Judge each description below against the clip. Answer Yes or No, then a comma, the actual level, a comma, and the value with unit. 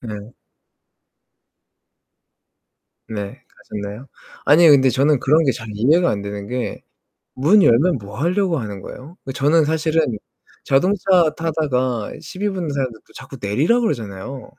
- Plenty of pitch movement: Yes, wide, 6.5 semitones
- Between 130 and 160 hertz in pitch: Yes, low, 135 Hz